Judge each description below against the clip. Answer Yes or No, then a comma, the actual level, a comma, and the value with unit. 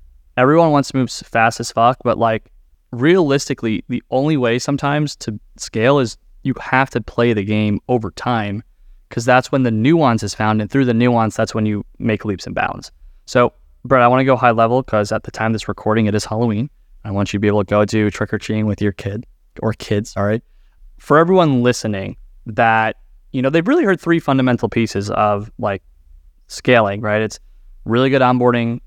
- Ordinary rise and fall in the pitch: Yes, average, 3.3 semitones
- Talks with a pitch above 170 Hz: No, low, 115 Hz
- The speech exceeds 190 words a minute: Yes, fast, 205 wpm